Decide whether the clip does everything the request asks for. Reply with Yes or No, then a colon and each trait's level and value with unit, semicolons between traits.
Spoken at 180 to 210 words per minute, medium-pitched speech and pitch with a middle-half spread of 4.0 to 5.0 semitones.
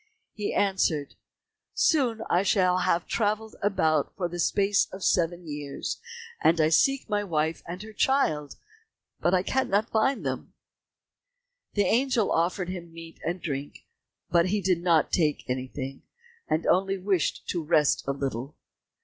No: average, 145 wpm; medium, 180 Hz; average, 4.6 semitones